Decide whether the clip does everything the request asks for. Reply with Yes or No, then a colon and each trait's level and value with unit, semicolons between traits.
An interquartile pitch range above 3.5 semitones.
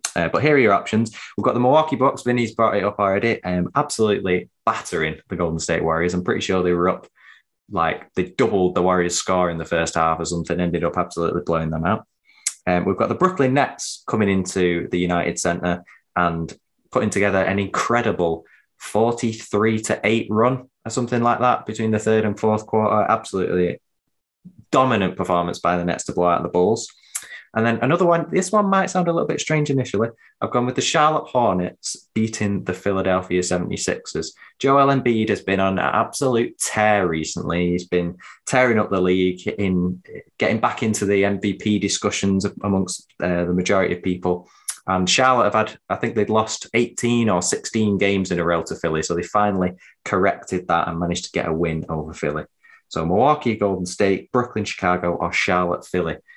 Yes: average, 4.1 semitones